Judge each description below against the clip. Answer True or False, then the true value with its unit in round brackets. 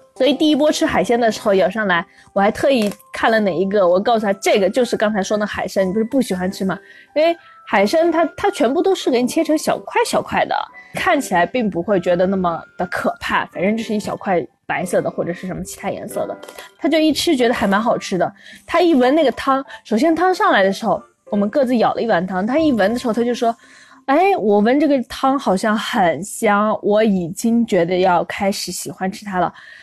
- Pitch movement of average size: False (7.4 semitones)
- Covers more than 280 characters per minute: True (330 characters per minute)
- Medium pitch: False (225 Hz)